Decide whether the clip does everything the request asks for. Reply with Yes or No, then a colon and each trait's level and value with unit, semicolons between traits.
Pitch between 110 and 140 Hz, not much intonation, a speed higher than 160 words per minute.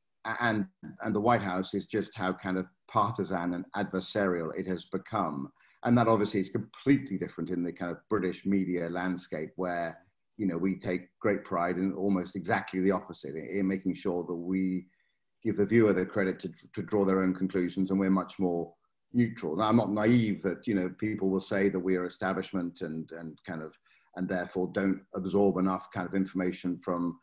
No: very low, 95 Hz; narrow, 1.8 semitones; average, 200 wpm